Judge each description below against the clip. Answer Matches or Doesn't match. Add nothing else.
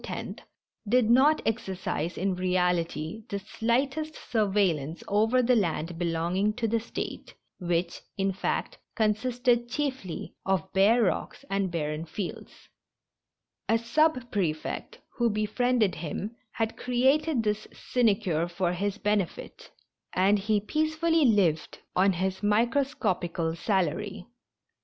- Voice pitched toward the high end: Matches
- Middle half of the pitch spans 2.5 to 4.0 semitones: Doesn't match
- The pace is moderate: Doesn't match